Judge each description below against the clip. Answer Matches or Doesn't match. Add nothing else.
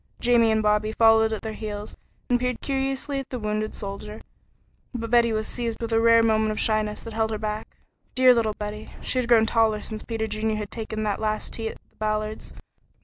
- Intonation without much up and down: Matches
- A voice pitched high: Matches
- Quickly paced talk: Matches